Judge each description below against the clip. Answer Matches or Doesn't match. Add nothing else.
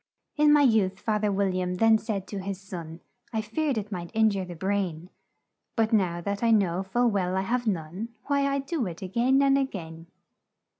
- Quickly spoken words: Matches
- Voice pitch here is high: Matches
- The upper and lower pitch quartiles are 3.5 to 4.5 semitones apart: Matches